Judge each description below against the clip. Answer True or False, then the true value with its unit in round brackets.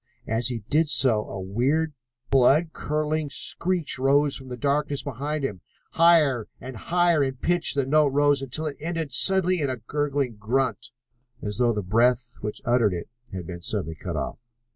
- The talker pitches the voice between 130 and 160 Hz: True (135 Hz)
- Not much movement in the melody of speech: False (4.4 semitones)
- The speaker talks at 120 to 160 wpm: False (175 wpm)